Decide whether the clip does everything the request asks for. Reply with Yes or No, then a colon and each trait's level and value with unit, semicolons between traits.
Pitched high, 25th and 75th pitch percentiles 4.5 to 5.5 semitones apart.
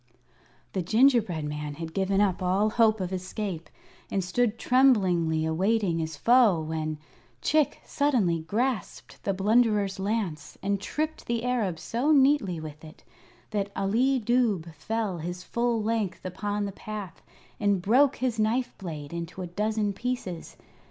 Yes: high, 200 Hz; average, 5.1 semitones